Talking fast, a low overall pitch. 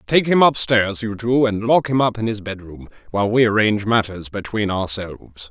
No: average, 195 wpm; low, 110 Hz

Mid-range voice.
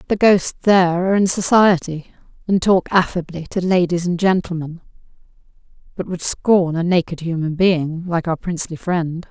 Yes: medium, 175 Hz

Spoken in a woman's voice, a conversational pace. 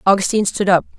Yes: female; average, 180 wpm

